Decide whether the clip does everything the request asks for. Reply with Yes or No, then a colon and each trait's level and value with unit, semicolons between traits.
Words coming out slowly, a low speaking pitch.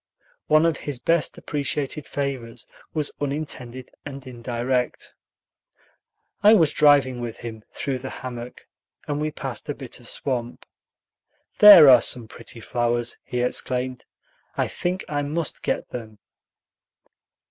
Yes: slow, 130 wpm; low, 130 Hz